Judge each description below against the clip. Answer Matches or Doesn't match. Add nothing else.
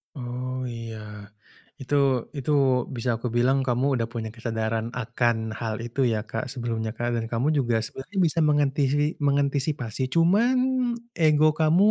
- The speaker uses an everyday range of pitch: Matches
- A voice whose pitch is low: Matches